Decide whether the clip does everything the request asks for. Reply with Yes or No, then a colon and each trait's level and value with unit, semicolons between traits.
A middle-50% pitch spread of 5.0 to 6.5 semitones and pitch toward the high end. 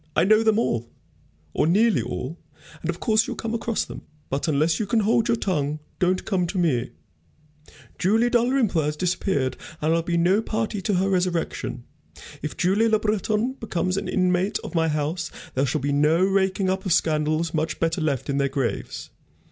No: average, 5.3 semitones; medium, 180 Hz